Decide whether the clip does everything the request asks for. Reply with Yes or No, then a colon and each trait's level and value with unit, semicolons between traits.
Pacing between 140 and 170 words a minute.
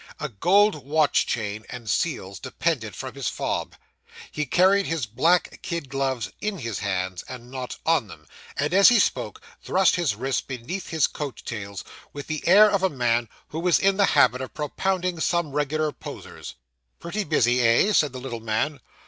No: average, 180 wpm